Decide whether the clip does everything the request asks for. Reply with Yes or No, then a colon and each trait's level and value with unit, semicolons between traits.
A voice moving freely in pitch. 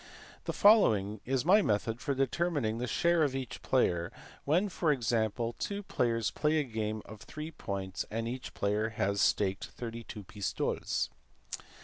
Yes: wide, 6.0 semitones